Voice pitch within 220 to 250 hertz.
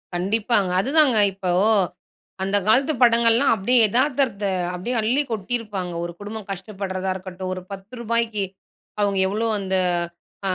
No: high, 210 Hz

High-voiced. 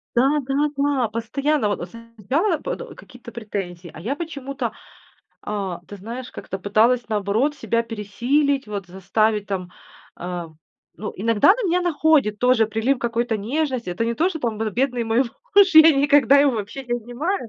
Yes: high, 235 Hz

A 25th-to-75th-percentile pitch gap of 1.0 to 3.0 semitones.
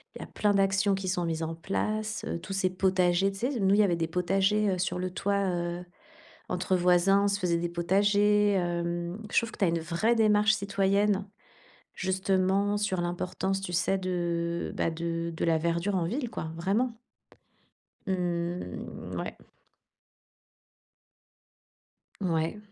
Yes: average, 2.7 semitones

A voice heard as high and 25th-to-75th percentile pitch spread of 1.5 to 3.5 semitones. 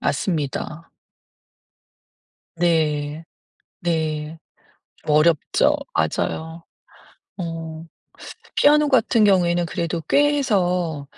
No: medium, 165 Hz; narrow, 2.5 semitones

